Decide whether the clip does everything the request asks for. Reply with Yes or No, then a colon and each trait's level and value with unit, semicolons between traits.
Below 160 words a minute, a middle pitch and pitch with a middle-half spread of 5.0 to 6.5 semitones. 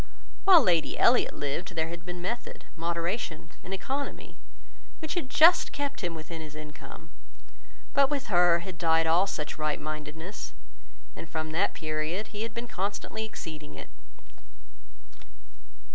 Yes: average, 145 wpm; medium, 175 Hz; wide, 5.5 semitones